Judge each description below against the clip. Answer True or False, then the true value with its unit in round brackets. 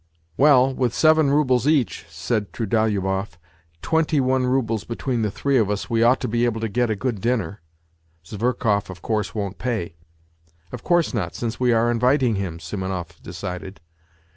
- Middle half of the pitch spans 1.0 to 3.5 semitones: False (4.7 semitones)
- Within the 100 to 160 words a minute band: False (180 wpm)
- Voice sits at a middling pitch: False (115 Hz)